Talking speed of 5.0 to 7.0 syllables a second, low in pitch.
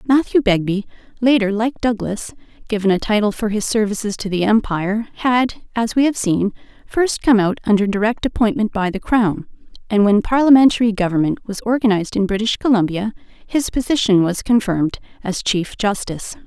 No: 5.4 syllables/s; high, 215 Hz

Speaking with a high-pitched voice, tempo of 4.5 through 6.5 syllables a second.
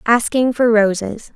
No: high, 225 Hz; 4.1 syllables/s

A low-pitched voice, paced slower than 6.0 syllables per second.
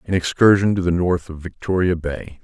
Yes: very low, 90 Hz; 5.2 syllables/s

